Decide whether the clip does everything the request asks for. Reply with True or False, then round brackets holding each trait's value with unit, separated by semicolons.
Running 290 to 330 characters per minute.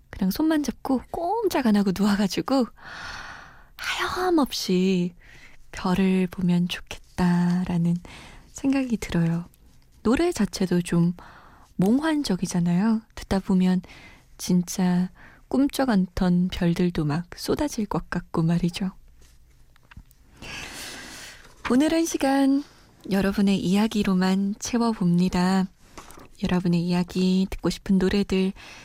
False (215 characters per minute)